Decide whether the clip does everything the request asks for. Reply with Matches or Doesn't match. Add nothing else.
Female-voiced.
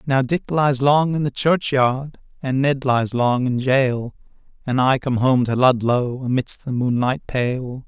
Doesn't match